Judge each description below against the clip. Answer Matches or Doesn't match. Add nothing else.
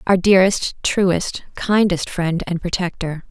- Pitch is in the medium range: Matches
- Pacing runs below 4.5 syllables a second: Matches